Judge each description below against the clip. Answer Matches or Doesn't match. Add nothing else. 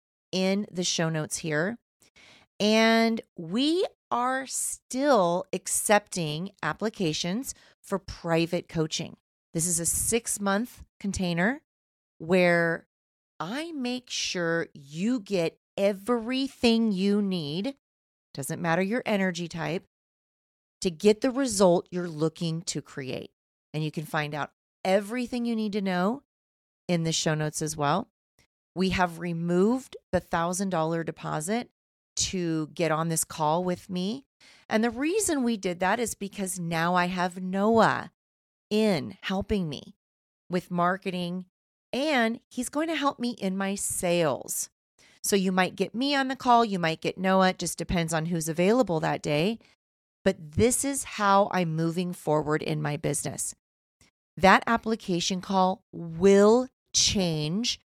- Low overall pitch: Doesn't match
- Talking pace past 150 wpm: Doesn't match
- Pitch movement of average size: Matches